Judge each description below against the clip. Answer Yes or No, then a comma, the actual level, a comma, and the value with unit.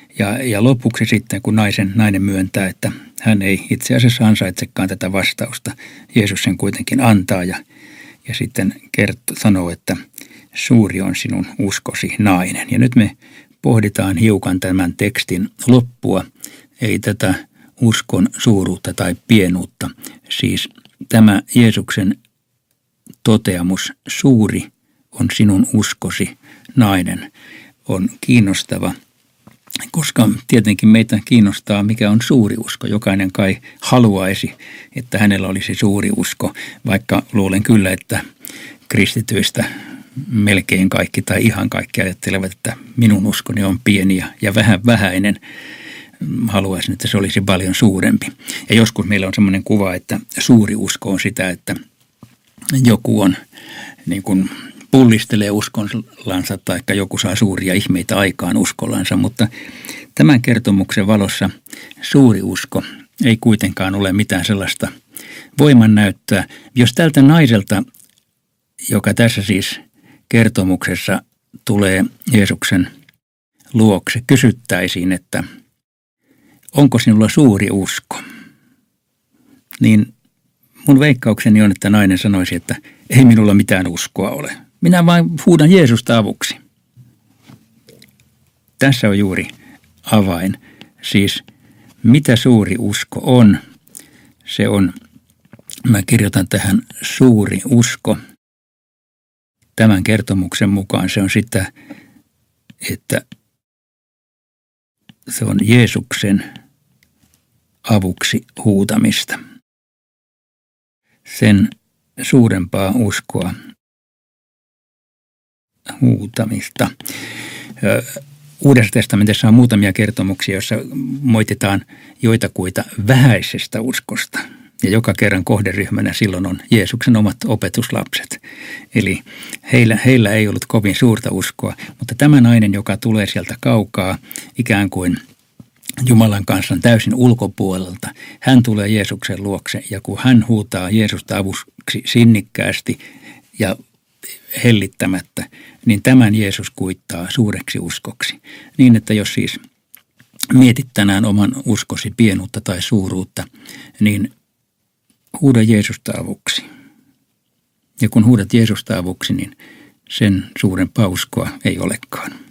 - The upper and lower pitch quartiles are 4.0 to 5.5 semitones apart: No, average, 3.5 semitones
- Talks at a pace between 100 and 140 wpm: Yes, average, 105 wpm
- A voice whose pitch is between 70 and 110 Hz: Yes, low, 105 Hz